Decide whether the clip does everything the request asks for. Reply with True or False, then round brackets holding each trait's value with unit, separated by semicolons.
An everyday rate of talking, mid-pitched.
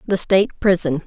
True (170 wpm; 180 Hz)